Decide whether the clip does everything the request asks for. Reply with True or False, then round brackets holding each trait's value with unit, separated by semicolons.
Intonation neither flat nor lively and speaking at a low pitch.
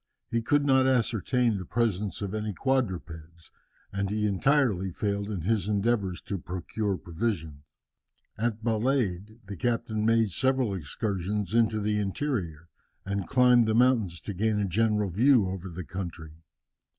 True (3.8 semitones; 105 Hz)